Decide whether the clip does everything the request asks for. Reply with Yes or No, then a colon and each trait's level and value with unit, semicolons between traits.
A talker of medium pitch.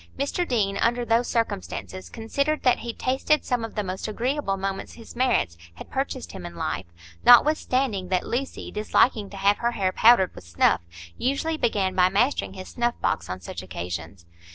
No: high, 220 Hz